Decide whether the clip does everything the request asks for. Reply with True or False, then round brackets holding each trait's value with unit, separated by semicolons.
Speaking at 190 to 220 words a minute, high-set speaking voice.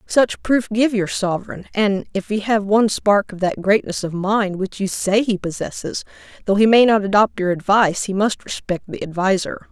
True (205 wpm; 200 Hz)